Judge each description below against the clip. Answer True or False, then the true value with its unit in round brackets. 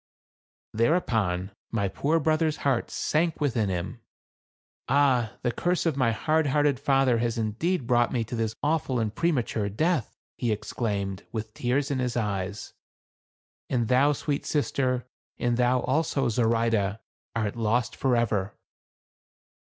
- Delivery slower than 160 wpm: True (140 wpm)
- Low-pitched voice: True (120 Hz)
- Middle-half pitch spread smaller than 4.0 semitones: False (4.3 semitones)